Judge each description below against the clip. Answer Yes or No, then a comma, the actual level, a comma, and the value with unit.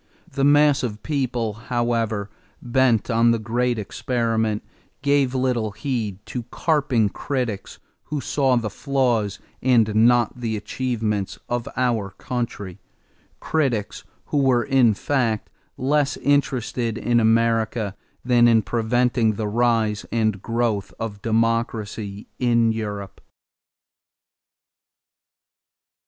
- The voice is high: No, low, 115 Hz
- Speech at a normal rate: No, slow, 110 wpm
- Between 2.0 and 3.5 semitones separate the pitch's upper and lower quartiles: Yes, narrow, 2.6 semitones